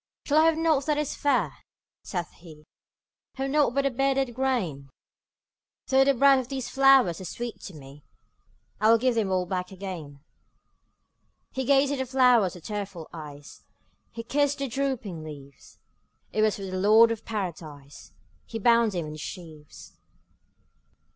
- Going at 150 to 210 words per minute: Yes, average, 165 wpm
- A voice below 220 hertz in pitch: No, high, 225 Hz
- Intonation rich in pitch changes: Yes, wide, 7.6 semitones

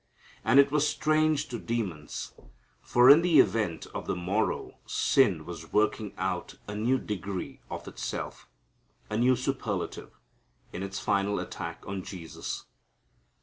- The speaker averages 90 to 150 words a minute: Yes, average, 140 wpm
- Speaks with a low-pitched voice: Yes, low, 105 Hz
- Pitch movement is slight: No, wide, 5.6 semitones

